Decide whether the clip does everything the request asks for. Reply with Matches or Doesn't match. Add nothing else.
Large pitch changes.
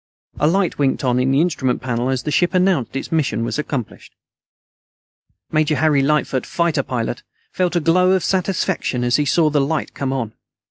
Doesn't match